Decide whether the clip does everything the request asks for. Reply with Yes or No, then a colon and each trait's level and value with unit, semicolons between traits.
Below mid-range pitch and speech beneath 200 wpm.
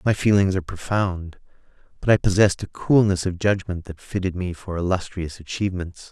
Yes: very low, 95 Hz; average, 165 wpm